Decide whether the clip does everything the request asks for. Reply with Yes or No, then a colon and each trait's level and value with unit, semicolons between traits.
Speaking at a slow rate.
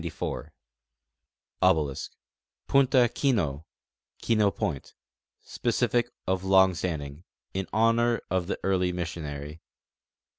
Yes: slow, 85 wpm